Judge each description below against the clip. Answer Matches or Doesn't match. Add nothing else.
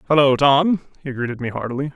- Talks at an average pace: Matches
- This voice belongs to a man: Matches